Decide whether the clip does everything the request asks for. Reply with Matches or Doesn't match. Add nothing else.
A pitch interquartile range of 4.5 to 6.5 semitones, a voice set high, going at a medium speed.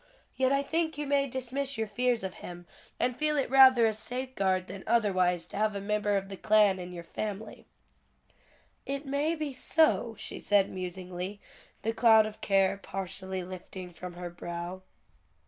Matches